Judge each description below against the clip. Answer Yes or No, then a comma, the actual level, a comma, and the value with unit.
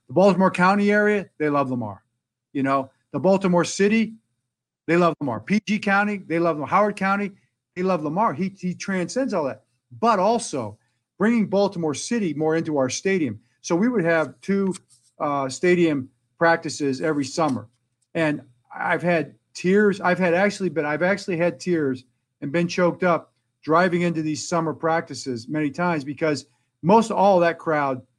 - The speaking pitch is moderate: Yes, medium, 165 Hz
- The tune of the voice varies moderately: No, wide, 5.7 semitones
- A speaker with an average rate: Yes, average, 165 wpm